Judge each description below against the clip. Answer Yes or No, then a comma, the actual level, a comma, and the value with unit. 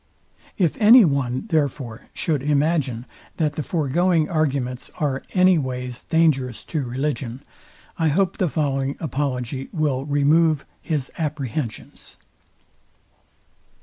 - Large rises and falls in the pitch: No, average, 3.5 semitones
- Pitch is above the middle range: No, medium, 145 Hz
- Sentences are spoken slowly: Yes, slow, 110 wpm